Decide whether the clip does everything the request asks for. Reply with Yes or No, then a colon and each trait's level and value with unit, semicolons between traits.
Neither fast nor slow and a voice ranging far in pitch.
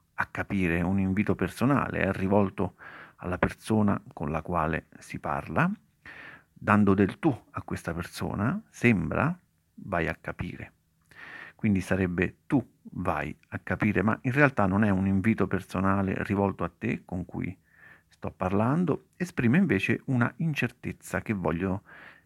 No: average, 140 wpm; average, 3.2 semitones